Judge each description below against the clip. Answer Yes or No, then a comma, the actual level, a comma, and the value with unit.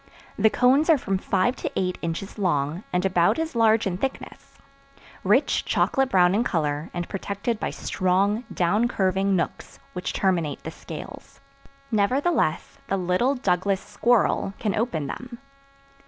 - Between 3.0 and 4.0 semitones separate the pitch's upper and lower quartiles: No, average, 4.8 semitones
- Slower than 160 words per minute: Yes, average, 145 wpm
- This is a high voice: Yes, high, 195 Hz